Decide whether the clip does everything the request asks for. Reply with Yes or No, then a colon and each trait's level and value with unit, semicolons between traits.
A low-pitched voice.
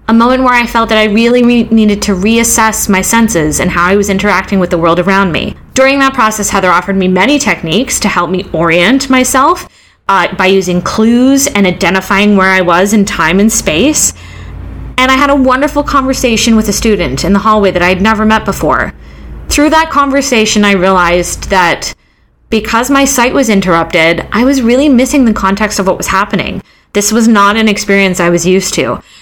No: high, 210 Hz